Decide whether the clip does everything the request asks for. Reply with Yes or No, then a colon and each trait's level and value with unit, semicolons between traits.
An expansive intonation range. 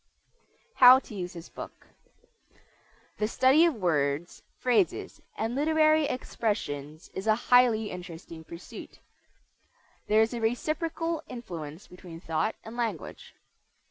Yes: wide, 6.8 semitones